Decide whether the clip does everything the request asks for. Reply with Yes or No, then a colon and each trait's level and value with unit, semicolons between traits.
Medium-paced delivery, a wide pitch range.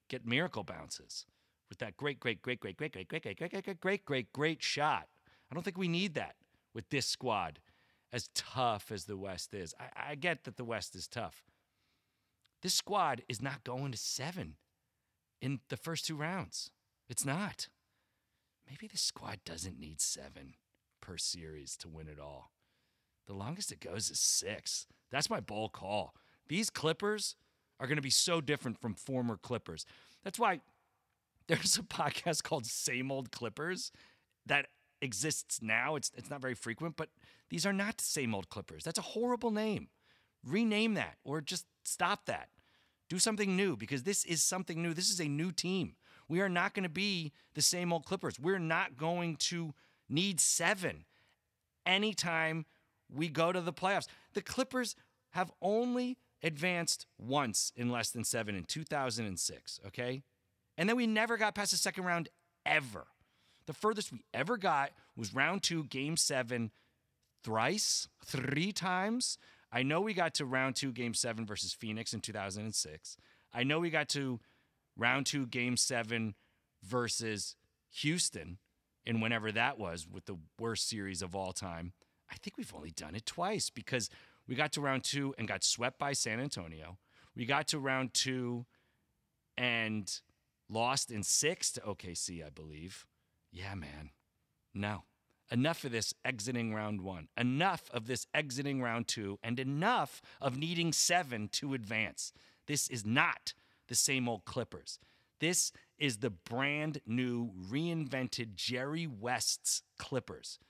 Yes: average, 160 wpm; wide, 7.0 semitones